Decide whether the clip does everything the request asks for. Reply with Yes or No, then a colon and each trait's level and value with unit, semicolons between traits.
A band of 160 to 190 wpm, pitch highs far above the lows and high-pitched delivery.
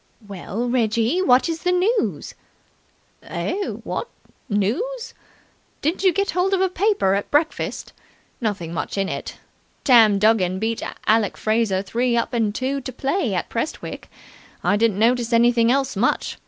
No: average, 150 wpm; wide, 7.5 semitones; high, 235 Hz